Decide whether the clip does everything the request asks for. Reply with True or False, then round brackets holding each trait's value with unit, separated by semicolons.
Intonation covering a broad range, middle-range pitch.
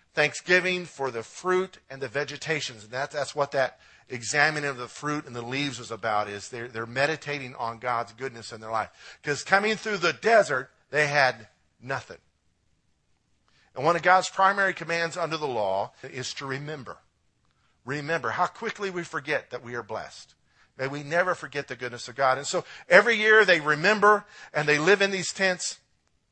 True (6.1 semitones; 145 Hz)